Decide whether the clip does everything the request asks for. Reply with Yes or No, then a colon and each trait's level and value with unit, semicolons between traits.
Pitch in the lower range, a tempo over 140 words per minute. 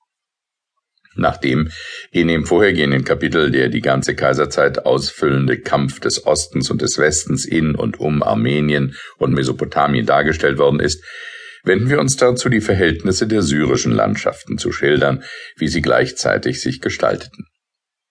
No: very low, 80 Hz; average, 135 wpm